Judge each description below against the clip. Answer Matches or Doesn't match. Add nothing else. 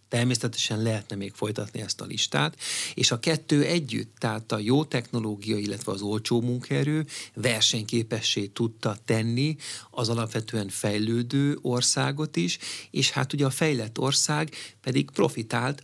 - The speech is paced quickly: Doesn't match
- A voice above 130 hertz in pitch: Doesn't match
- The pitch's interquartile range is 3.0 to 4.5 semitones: Matches